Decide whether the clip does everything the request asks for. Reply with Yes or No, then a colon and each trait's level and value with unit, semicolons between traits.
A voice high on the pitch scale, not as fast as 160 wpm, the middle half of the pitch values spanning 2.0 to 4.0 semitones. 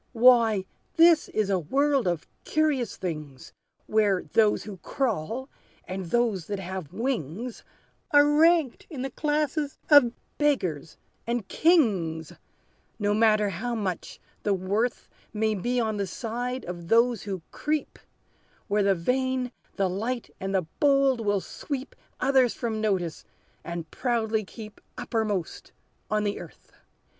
No: high, 220 Hz; slow, 135 wpm; average, 5.2 semitones